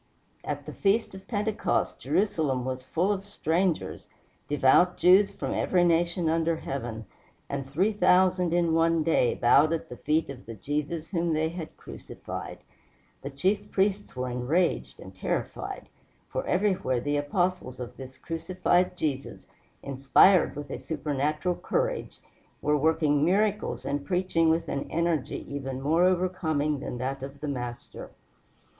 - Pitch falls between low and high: Yes, medium, 160 Hz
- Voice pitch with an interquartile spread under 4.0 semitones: No, average, 4.7 semitones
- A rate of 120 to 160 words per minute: Yes, average, 145 wpm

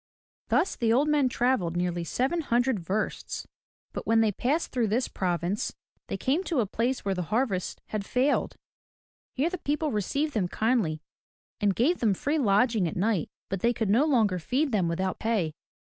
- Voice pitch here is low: No, high, 225 Hz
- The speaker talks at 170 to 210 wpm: Yes, average, 180 wpm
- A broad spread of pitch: Yes, wide, 5.7 semitones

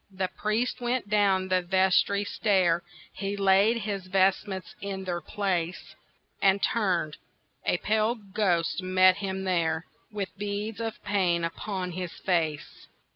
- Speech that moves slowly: Yes, slow, 130 wpm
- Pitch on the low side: No, high, 190 Hz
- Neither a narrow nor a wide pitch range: No, narrow, 2.2 semitones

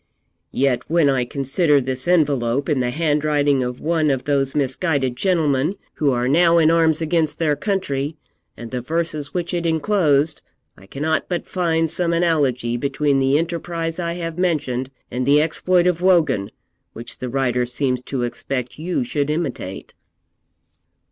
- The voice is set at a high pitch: No, medium, 150 Hz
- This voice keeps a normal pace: Yes, average, 155 wpm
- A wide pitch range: No, average, 4.0 semitones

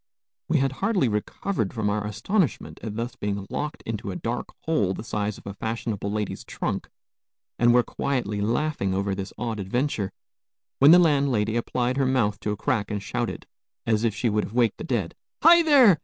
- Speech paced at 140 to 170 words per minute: No, average, 190 wpm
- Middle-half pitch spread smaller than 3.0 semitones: No, average, 4.7 semitones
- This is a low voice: Yes, low, 115 Hz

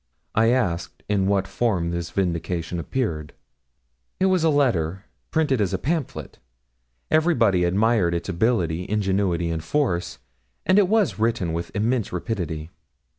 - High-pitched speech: No, low, 100 Hz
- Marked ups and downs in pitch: Yes, wide, 6.1 semitones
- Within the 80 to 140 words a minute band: Yes, slow, 135 wpm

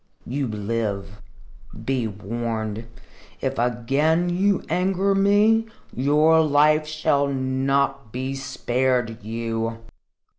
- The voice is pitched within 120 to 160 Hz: Yes, low, 135 Hz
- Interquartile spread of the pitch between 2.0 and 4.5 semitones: No, average, 4.9 semitones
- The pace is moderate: No, slow, 90 wpm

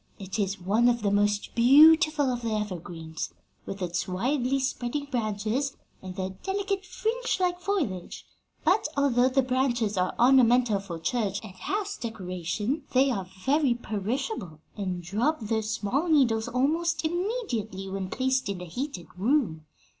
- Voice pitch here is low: No, high, 235 Hz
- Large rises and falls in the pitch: Yes, wide, 6.3 semitones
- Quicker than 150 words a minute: No, average, 145 wpm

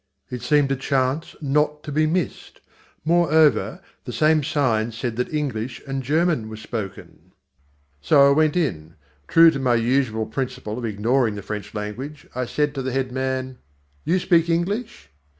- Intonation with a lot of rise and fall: No, average, 4.5 semitones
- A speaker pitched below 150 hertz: Yes, low, 135 Hz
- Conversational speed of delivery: Yes, average, 165 wpm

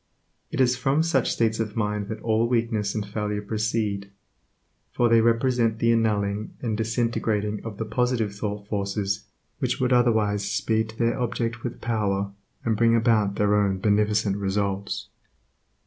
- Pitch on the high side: No, low, 110 Hz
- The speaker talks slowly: No, average, 155 wpm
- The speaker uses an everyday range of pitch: No, narrow, 2.1 semitones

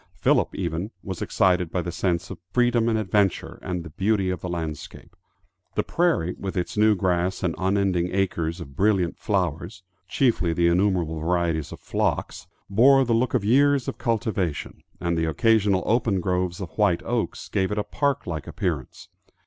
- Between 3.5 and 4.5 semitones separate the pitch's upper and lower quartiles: Yes, average, 3.9 semitones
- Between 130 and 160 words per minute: No, average, 175 wpm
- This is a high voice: No, very low, 95 Hz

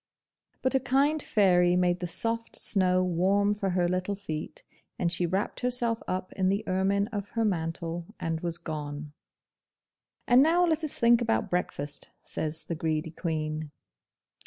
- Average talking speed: Yes, average, 160 wpm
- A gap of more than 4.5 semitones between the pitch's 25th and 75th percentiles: Yes, average, 5.3 semitones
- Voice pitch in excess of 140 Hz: Yes, medium, 185 Hz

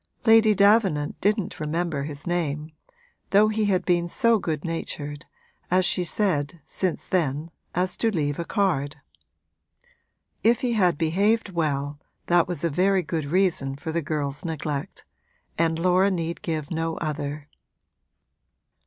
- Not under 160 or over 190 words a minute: No, average, 140 wpm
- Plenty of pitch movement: No, average, 4.0 semitones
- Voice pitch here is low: No, medium, 170 Hz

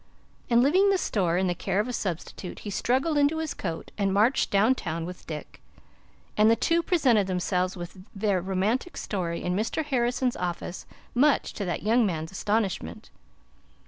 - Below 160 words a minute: No, average, 175 wpm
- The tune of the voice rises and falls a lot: Yes, wide, 5.7 semitones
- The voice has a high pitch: Yes, high, 205 Hz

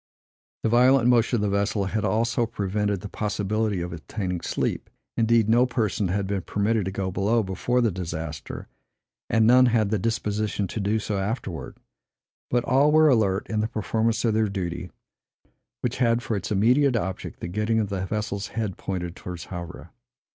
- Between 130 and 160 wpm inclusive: No, average, 175 wpm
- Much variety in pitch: No, average, 3.2 semitones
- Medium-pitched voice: No, low, 105 Hz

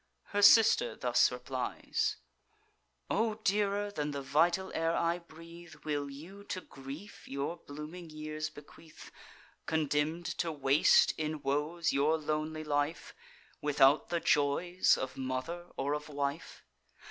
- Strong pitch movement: No, average, 3.0 semitones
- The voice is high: No, medium, 155 Hz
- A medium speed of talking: No, slow, 125 wpm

